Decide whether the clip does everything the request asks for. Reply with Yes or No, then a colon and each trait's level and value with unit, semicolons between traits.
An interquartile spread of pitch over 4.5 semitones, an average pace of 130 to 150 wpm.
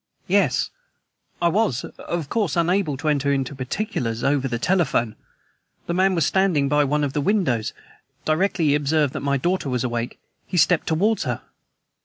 No: average, 5.0 semitones; average, 170 wpm